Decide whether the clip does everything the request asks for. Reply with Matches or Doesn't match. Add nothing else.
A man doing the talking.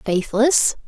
Doesn't match